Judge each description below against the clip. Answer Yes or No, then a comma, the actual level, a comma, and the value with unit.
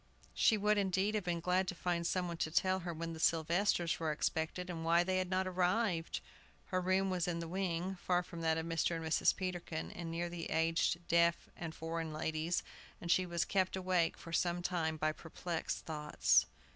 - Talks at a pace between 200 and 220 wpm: Yes, fast, 205 wpm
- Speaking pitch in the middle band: Yes, medium, 170 Hz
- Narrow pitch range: Yes, narrow, 1.9 semitones